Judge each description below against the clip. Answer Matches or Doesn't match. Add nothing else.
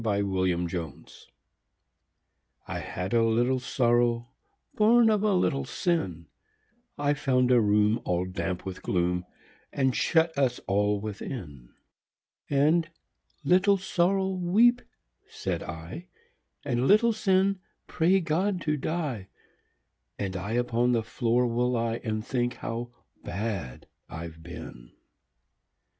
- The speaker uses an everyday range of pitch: Doesn't match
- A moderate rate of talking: Doesn't match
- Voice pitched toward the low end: Matches